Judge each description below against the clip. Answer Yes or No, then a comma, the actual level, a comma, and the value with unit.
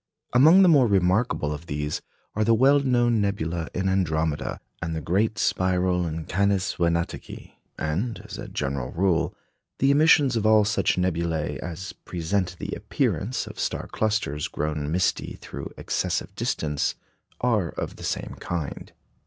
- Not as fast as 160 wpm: Yes, average, 150 wpm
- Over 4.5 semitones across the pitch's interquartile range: Yes, average, 5.1 semitones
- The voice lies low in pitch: Yes, very low, 90 Hz